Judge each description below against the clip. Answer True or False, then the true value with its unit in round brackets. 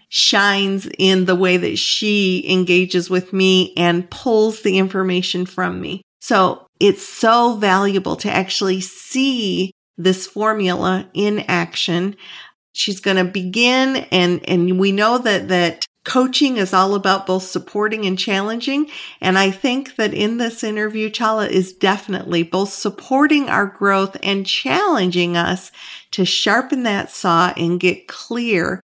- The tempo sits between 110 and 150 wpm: True (140 wpm)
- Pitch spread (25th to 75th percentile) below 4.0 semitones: True (2.8 semitones)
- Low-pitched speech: False (195 Hz)